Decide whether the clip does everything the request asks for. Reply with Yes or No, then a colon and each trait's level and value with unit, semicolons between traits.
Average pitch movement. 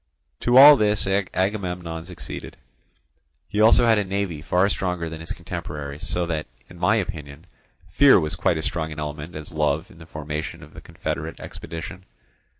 Yes: average, 3.8 semitones